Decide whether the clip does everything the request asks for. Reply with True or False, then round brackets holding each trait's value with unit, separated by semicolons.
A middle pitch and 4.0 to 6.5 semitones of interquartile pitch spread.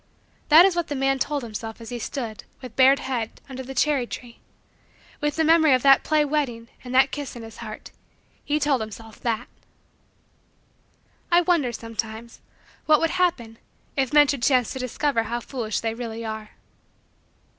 False (255 Hz; 4.3 semitones)